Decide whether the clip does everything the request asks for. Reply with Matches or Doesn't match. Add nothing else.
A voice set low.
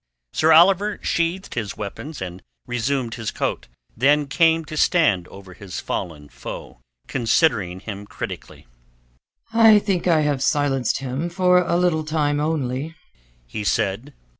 Doesn't match